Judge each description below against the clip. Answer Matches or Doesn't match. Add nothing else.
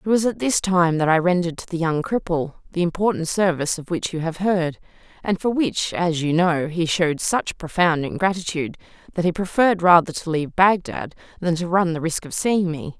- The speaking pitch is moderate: Matches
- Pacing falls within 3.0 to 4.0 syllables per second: Doesn't match